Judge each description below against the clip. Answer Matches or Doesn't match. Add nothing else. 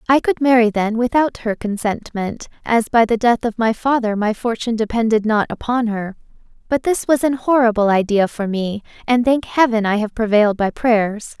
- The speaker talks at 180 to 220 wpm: Matches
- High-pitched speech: Matches